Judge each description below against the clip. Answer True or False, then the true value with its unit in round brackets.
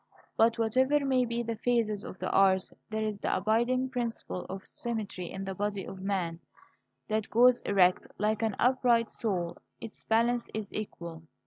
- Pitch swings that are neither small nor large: True (3.6 semitones)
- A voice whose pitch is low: False (220 Hz)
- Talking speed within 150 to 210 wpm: True (165 wpm)